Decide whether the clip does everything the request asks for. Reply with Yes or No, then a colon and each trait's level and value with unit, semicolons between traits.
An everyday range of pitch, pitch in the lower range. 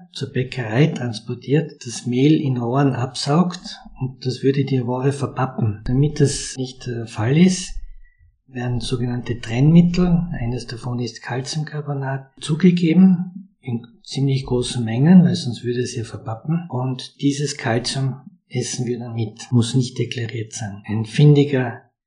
Yes: average, 3.5 semitones; low, 130 Hz